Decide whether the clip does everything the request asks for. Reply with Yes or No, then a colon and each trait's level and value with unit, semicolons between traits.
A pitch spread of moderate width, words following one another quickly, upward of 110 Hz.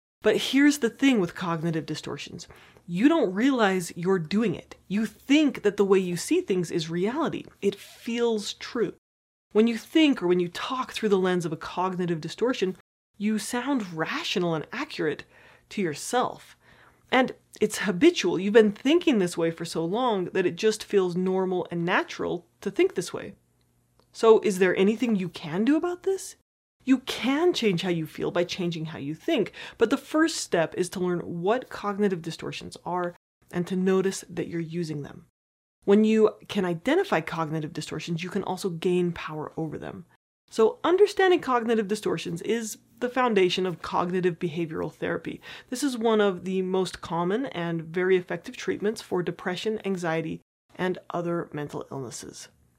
No: average, 5.0 semitones; average, 170 wpm; high, 190 Hz